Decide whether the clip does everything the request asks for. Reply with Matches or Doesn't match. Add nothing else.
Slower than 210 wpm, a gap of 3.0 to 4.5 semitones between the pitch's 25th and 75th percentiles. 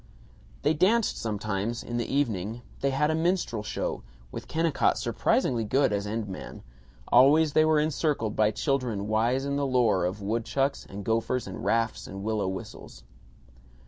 Doesn't match